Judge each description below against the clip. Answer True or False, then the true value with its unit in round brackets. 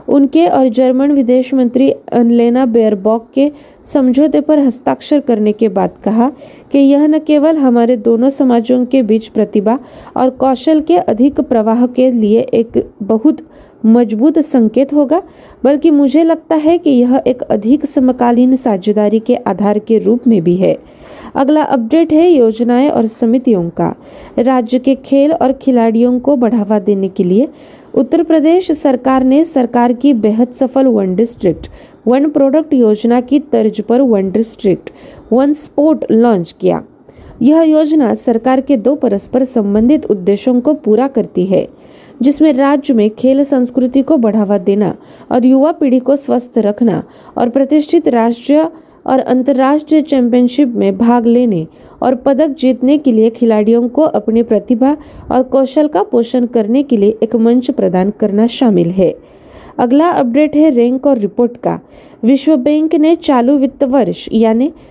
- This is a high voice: True (255 Hz)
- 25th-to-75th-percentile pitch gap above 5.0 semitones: False (3.9 semitones)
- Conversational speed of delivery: False (150 wpm)